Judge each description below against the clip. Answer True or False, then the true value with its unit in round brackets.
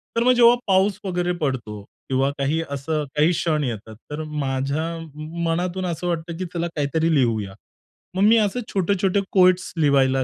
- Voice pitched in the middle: True (160 Hz)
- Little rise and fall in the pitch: False (5.0 semitones)